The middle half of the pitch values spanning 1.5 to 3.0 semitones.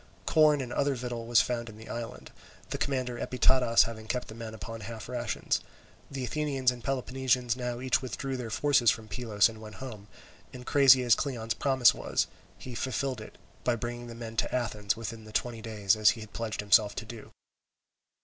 Yes: narrow, 2.5 semitones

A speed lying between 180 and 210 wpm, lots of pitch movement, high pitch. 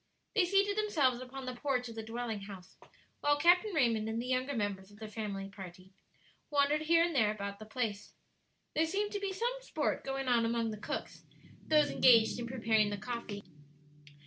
Yes: average, 190 wpm; wide, 5.7 semitones; high, 240 Hz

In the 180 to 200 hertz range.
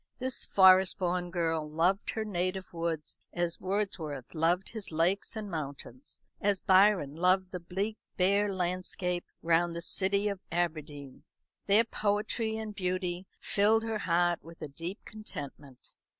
Yes: medium, 185 Hz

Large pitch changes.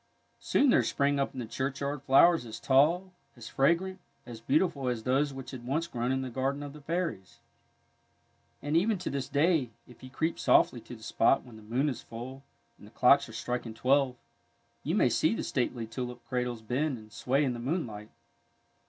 No: average, 3.3 semitones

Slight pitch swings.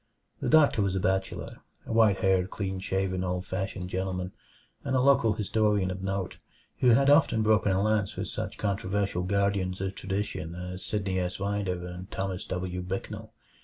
Yes: narrow, 2.0 semitones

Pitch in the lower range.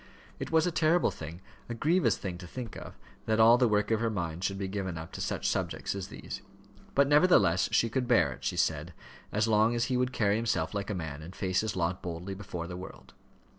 Yes: low, 105 Hz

